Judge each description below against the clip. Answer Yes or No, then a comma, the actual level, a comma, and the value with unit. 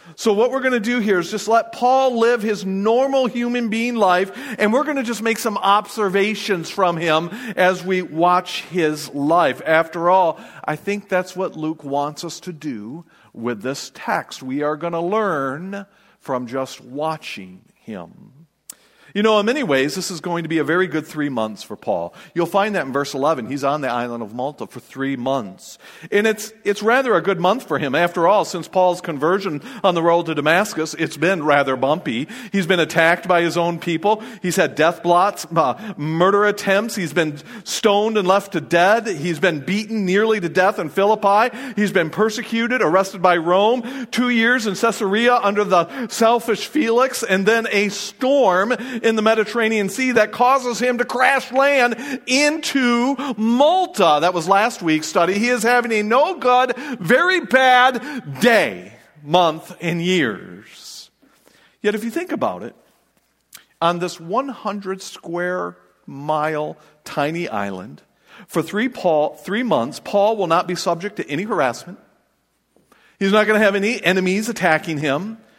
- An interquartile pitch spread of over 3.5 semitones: Yes, wide, 5.4 semitones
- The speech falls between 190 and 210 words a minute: No, average, 170 wpm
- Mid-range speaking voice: No, high, 195 Hz